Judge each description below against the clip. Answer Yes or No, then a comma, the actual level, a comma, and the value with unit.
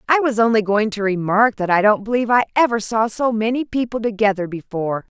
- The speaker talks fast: Yes, fast, 210 wpm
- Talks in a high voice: Yes, high, 220 Hz